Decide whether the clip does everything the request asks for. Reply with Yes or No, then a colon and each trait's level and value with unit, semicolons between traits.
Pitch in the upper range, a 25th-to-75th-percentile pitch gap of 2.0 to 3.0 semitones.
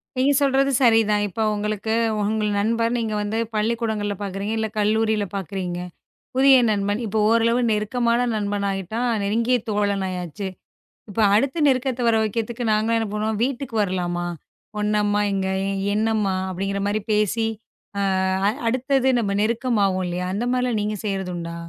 Yes: high, 215 Hz; narrow, 2.5 semitones